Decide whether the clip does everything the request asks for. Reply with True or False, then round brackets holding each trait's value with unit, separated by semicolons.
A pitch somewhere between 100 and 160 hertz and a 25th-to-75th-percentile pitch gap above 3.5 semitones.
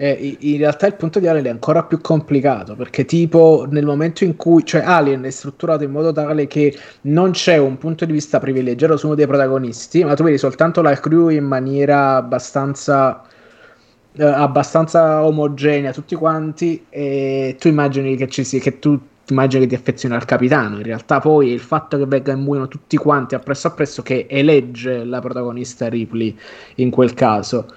False (140 Hz; 2.9 semitones)